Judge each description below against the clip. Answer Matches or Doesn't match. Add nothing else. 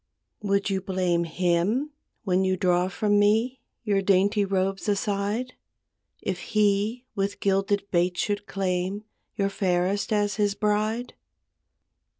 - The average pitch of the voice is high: Matches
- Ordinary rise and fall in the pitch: Doesn't match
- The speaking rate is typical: Doesn't match